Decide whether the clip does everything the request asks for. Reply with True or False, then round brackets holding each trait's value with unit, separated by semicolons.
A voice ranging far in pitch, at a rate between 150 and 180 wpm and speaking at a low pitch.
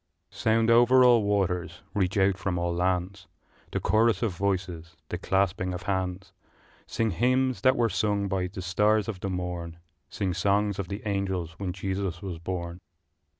False (2.5 semitones; 170 wpm; 95 Hz)